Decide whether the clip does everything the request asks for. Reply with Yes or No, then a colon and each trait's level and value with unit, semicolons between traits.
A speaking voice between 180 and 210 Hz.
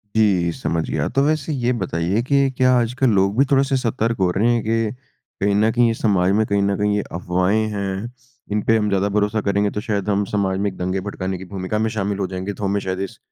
No: low, 105 Hz